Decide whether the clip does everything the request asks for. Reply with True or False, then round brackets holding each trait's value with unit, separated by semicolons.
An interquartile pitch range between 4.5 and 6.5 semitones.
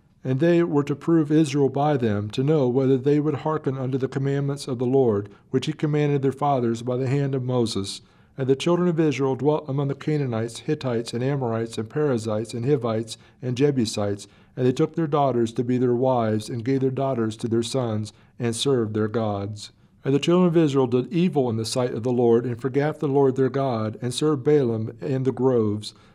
False (3.8 semitones)